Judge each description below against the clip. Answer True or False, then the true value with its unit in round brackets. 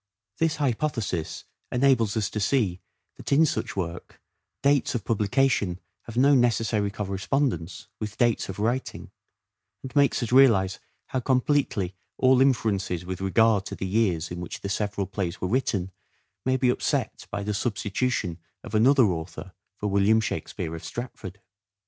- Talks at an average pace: True (150 wpm)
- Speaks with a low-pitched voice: True (110 Hz)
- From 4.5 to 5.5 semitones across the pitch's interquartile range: True (5.1 semitones)